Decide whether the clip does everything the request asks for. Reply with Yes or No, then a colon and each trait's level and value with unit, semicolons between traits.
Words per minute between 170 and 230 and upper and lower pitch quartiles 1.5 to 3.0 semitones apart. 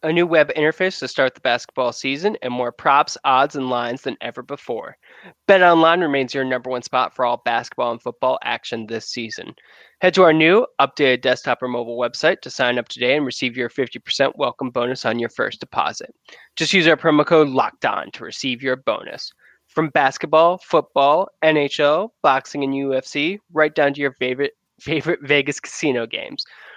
No: average, 185 wpm; average, 4.1 semitones